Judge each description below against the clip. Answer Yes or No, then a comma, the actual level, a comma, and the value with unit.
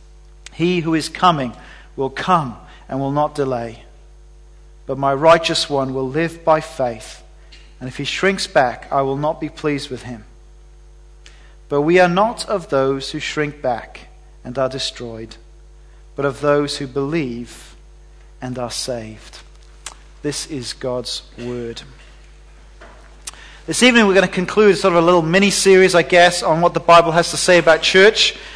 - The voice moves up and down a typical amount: No, wide, 5.7 semitones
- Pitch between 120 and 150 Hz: Yes, medium, 140 Hz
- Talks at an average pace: Yes, average, 160 wpm